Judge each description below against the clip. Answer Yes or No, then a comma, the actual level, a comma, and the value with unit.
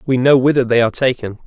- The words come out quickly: Yes, fast, 245 wpm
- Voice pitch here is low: Yes, low, 125 Hz